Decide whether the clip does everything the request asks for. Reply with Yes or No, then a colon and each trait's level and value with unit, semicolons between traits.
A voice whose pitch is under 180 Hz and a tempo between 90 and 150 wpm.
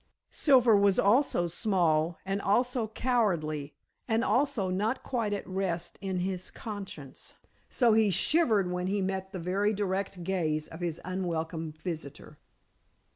No: high, 190 Hz; slow, 135 wpm